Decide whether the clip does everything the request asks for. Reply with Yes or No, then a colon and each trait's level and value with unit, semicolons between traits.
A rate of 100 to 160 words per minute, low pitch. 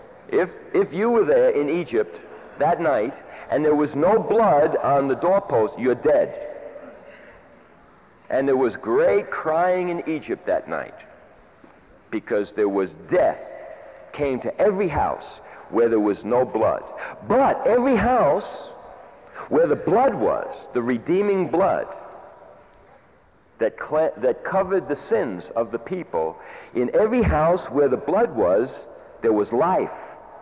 No: average, 140 wpm; medium, 175 Hz